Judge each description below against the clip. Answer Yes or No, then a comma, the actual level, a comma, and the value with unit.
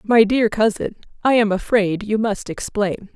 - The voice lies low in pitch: No, high, 215 Hz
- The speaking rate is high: No, average, 170 wpm